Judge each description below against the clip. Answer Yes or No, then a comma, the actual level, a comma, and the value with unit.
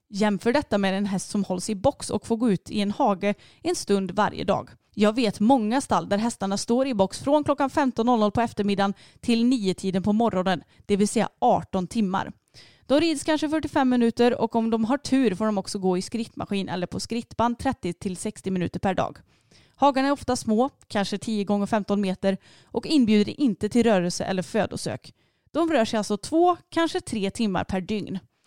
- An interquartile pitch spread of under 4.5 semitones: Yes, average, 4.0 semitones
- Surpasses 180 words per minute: Yes, average, 190 wpm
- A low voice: No, high, 215 Hz